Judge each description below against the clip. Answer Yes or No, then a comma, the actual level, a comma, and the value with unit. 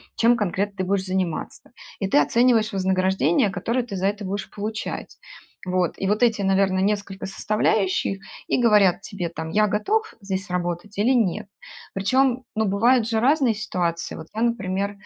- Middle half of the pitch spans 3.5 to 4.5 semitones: No, average, 2.9 semitones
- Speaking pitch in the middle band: No, high, 200 Hz